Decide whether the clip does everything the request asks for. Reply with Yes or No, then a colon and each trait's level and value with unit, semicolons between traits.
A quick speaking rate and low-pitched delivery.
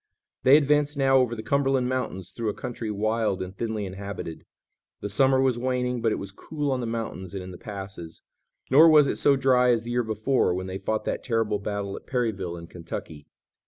Yes: fast, 210 wpm; low, 115 Hz